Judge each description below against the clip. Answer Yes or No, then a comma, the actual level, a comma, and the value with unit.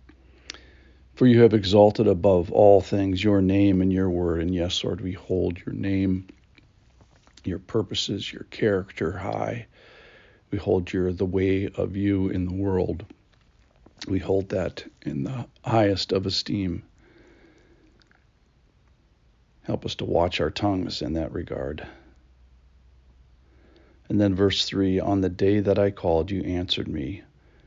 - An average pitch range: Yes, average, 3.5 semitones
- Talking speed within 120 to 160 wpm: Yes, average, 140 wpm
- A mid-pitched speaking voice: No, very low, 95 Hz